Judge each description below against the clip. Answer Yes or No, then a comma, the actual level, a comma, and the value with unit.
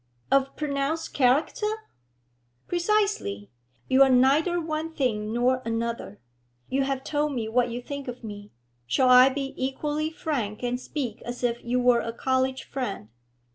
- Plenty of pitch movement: No, average, 3.6 semitones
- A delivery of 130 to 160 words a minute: Yes, average, 150 wpm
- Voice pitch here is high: Yes, very high, 260 Hz